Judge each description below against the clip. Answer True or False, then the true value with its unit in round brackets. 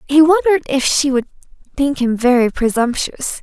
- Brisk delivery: False (160 wpm)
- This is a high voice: True (270 Hz)